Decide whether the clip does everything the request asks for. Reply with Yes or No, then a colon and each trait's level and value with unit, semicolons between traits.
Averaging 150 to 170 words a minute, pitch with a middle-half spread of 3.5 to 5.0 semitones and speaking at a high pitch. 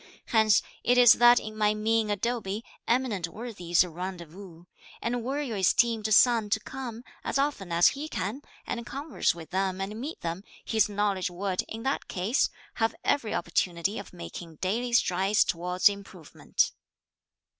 Yes: average, 155 wpm; average, 4.4 semitones; high, 210 Hz